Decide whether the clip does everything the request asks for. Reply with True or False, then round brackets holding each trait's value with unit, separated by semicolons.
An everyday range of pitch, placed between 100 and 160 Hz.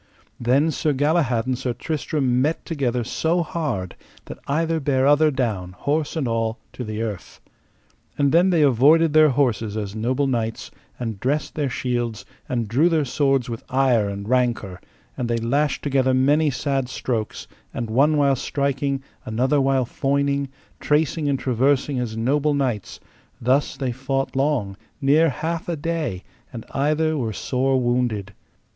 True (3.7 semitones; 135 Hz)